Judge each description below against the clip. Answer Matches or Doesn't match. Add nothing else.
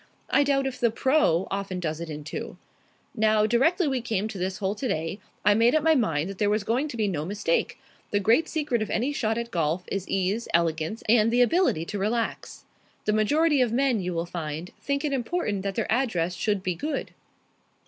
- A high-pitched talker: Matches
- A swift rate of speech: Matches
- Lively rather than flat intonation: Matches